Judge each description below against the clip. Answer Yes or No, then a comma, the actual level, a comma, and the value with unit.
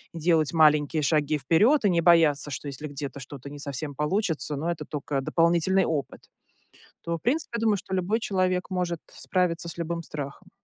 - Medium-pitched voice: Yes, medium, 165 Hz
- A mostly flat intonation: No, average, 3.7 semitones